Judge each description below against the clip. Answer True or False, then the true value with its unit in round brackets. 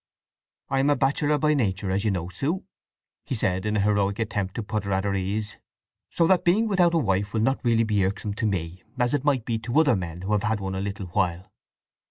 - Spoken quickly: True (245 wpm)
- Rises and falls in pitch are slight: False (5.6 semitones)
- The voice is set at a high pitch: False (105 Hz)